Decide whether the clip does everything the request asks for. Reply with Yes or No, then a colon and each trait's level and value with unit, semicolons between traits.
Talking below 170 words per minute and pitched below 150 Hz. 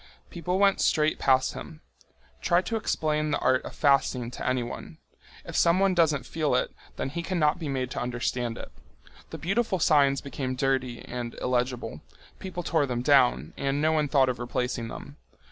No: average, 175 wpm; medium, 140 Hz